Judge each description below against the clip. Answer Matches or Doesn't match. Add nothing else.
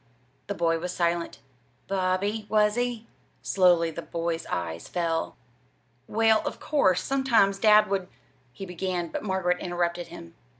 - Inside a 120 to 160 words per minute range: Matches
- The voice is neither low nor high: Matches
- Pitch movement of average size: Matches